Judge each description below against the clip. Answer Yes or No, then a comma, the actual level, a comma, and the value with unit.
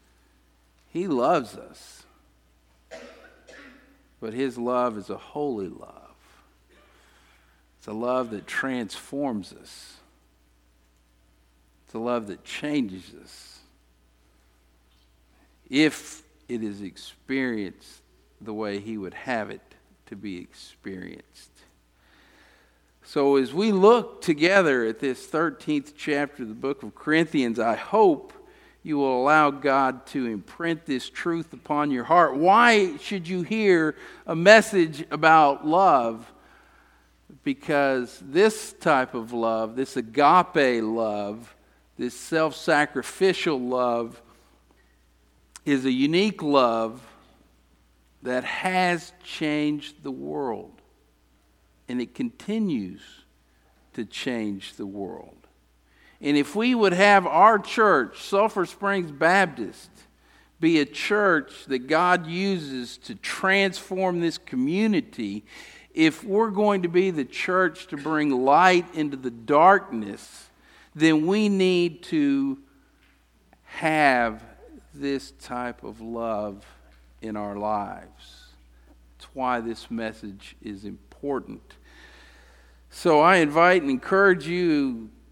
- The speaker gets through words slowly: Yes, slow, 110 wpm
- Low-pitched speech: Yes, low, 130 Hz